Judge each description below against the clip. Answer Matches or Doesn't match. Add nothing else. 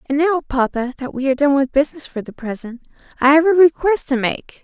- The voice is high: Matches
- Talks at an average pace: Doesn't match